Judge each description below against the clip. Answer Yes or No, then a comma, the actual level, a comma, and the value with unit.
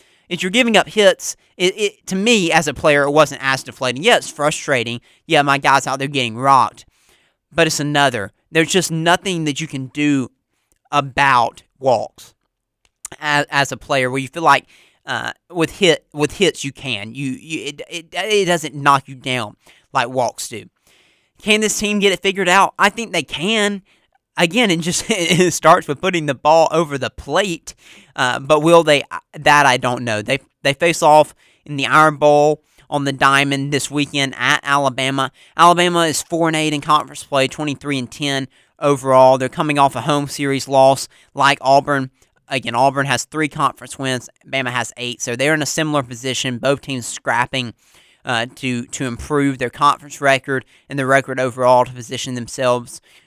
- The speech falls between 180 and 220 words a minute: Yes, average, 185 wpm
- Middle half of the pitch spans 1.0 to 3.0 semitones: No, average, 3.5 semitones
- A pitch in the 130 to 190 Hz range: Yes, medium, 140 Hz